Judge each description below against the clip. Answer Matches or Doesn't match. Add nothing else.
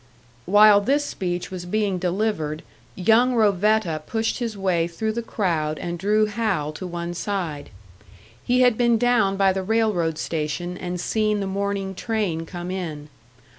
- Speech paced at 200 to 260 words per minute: Doesn't match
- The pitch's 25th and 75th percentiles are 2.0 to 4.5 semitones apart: Matches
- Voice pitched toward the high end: Matches